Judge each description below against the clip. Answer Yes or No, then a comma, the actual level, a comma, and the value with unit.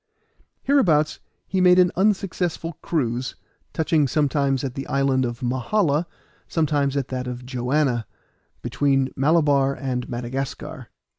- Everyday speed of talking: No, slow, 120 wpm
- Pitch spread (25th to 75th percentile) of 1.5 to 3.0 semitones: No, average, 3.8 semitones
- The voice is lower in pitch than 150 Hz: Yes, medium, 140 Hz